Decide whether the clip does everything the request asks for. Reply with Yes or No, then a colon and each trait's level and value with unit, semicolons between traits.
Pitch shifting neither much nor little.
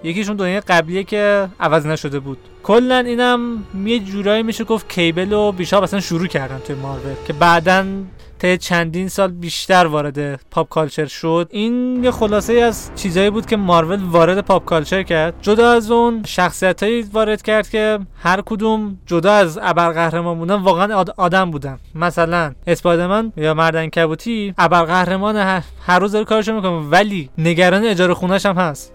Yes: average, 3.8 semitones